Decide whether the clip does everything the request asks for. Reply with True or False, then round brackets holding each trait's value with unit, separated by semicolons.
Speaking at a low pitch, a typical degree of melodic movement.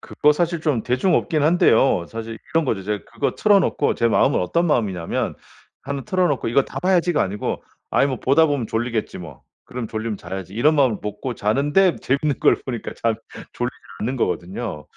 False (125 Hz; 5.9 semitones)